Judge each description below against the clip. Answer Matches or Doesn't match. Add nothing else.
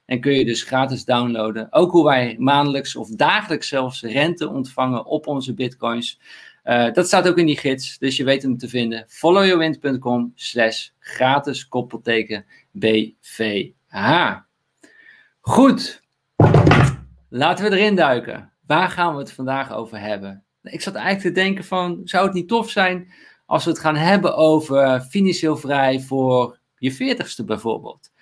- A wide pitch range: Matches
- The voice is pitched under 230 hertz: Matches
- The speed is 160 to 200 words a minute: Doesn't match